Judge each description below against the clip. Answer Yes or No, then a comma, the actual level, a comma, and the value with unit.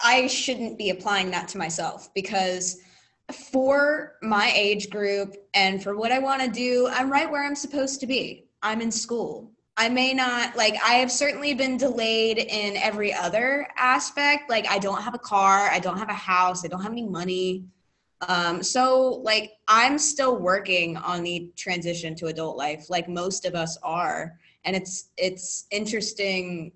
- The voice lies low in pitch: No, high, 210 Hz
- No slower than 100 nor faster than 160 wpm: No, average, 175 wpm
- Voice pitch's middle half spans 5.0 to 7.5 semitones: Yes, wide, 5.6 semitones